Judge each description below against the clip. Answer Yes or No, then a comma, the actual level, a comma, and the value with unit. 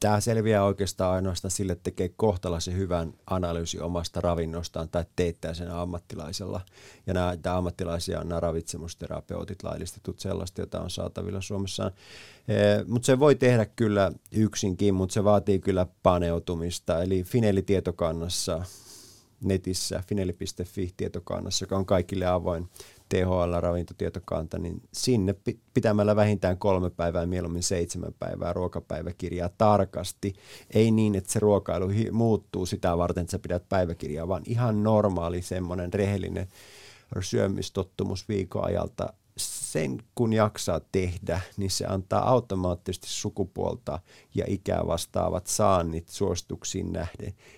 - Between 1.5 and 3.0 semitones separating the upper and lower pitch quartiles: Yes, narrow, 2.6 semitones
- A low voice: Yes, very low, 95 Hz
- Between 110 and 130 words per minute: Yes, average, 120 wpm